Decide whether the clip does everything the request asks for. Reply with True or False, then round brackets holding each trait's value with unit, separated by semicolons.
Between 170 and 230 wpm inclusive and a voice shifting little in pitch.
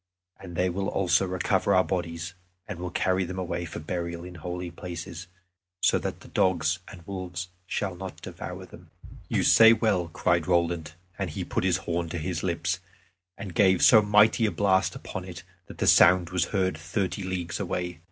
True (185 wpm; 1.7 semitones)